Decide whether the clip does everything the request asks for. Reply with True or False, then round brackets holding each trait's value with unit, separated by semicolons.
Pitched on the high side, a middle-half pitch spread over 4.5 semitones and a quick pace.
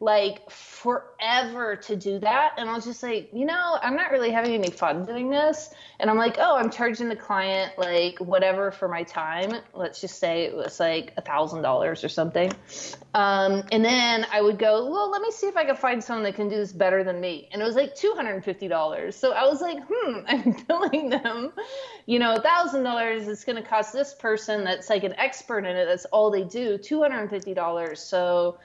True (220 Hz; 5.5 semitones; 230 wpm)